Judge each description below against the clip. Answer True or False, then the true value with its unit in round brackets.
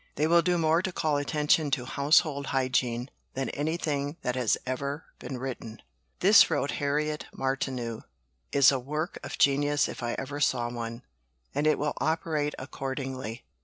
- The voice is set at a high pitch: False (140 Hz)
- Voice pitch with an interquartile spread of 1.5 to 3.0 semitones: True (2.7 semitones)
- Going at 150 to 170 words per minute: True (160 wpm)